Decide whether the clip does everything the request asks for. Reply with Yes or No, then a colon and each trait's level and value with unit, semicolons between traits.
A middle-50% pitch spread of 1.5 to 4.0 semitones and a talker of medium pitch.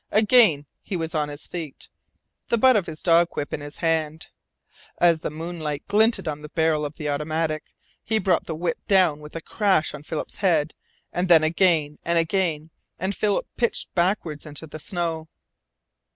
Yes: average, 3.1 semitones; medium, 165 Hz